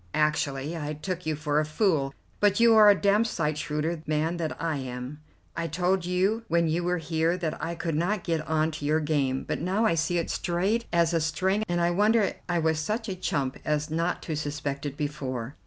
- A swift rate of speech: Yes, fast, 220 wpm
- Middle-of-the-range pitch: Yes, medium, 165 Hz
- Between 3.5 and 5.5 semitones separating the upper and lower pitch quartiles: No, average, 3.1 semitones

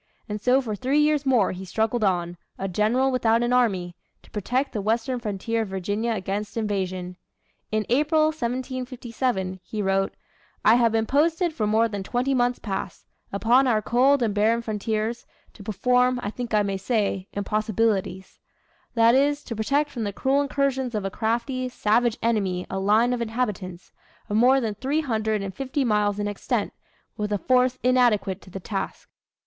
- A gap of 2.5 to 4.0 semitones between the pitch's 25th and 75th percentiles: Yes, average, 3.6 semitones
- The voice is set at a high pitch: Yes, high, 225 Hz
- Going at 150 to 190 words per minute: Yes, average, 175 wpm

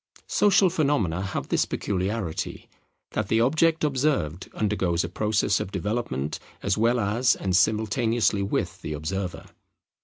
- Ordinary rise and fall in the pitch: Yes, average, 4.6 semitones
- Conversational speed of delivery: No, slow, 130 wpm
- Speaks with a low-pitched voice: Yes, low, 105 Hz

